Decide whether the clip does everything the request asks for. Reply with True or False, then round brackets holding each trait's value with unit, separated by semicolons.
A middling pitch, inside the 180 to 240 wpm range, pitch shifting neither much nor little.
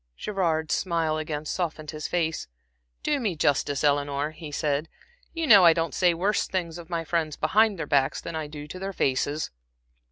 True (160 Hz; 185 wpm; 3.1 semitones)